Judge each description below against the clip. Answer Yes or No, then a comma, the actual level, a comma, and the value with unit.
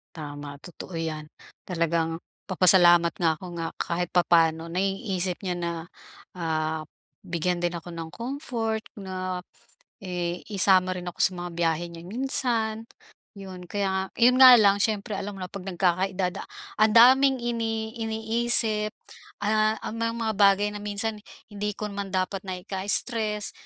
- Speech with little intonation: No, average, 3.9 semitones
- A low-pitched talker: No, high, 190 Hz